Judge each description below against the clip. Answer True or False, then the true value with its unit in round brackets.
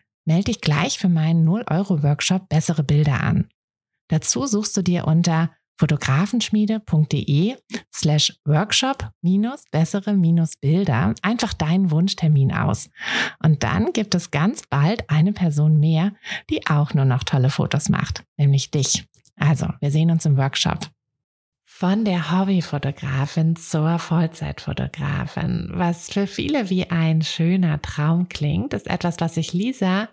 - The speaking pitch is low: False (165 Hz)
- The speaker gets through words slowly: False (135 wpm)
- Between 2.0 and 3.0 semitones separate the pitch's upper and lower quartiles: False (3.7 semitones)